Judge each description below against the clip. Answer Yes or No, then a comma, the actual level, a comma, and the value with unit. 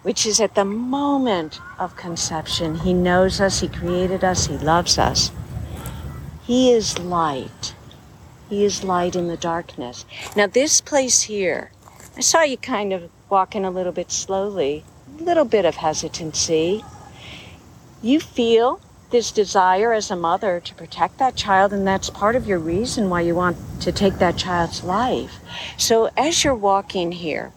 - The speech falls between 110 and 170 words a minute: Yes, average, 160 wpm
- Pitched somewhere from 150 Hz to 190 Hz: Yes, medium, 185 Hz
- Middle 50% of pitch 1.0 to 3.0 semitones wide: No, average, 4.3 semitones